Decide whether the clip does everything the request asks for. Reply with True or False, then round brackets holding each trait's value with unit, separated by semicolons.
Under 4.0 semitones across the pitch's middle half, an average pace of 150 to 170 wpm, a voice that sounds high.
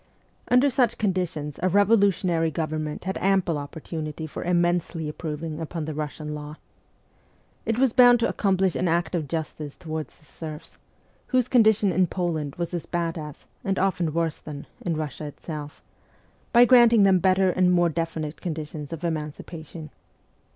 False (3.6 semitones; 155 wpm; 165 Hz)